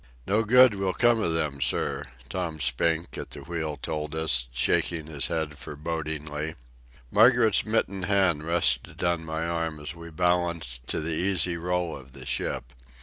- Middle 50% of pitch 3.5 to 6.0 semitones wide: No, average, 2.9 semitones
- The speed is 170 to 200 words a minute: No, average, 160 wpm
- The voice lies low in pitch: Yes, very low, 80 Hz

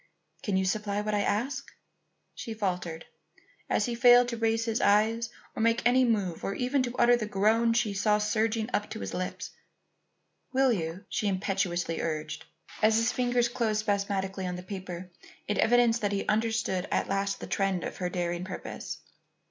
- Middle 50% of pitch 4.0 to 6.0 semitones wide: No, average, 3.2 semitones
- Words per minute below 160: No, average, 180 wpm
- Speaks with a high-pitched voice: Yes, high, 210 Hz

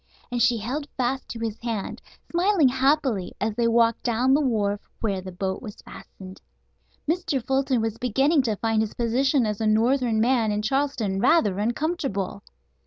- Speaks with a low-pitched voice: No, high, 235 Hz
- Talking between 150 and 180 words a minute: Yes, average, 170 wpm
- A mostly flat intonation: No, average, 4.0 semitones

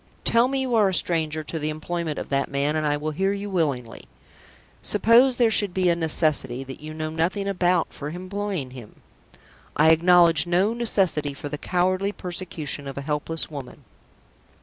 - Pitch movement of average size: Yes, average, 4.4 semitones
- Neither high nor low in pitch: Yes, medium, 165 Hz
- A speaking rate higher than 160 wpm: Yes, average, 180 wpm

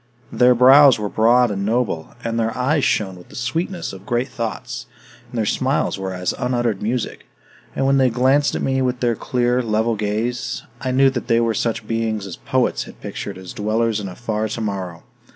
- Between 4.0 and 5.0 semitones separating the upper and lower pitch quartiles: No, average, 2.9 semitones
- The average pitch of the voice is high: No, low, 115 Hz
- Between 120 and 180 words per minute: No, average, 200 wpm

